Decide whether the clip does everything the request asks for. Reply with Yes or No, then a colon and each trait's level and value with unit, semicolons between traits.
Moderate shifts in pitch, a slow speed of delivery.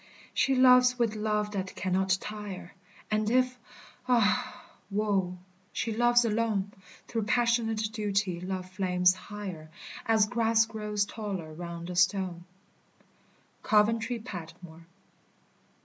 Yes: average, 3.6 semitones; slow, 110 wpm